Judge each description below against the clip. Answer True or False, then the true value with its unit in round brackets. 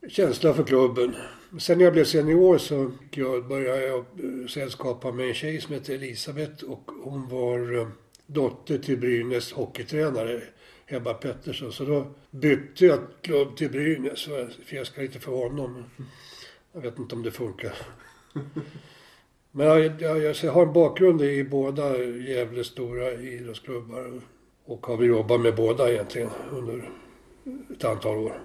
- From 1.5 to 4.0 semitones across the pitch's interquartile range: True (3.7 semitones)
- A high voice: False (135 Hz)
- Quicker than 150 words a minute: False (145 wpm)